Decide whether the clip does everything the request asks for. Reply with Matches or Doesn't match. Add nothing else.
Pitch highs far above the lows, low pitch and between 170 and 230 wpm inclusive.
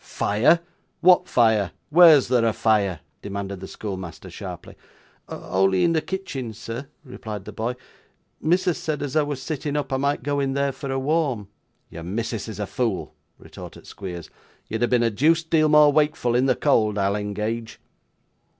Matches